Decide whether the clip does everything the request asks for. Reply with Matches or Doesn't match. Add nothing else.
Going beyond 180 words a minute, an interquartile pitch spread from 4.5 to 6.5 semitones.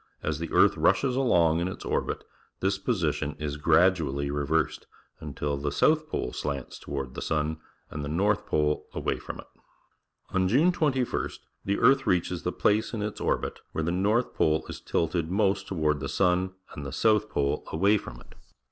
Matches